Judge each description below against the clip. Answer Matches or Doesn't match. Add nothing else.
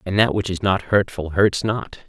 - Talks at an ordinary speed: Doesn't match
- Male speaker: Matches